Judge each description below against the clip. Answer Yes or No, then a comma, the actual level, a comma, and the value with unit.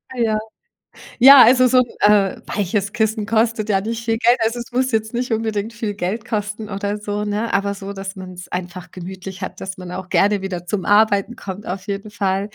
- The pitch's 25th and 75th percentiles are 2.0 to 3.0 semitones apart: Yes, narrow, 2.6 semitones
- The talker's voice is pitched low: No, high, 205 Hz